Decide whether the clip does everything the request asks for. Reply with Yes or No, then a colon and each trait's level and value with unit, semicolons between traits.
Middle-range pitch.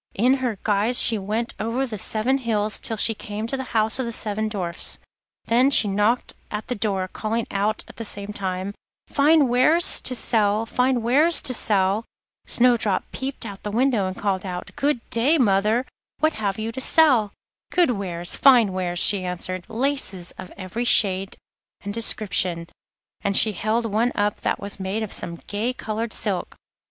No: high, 215 Hz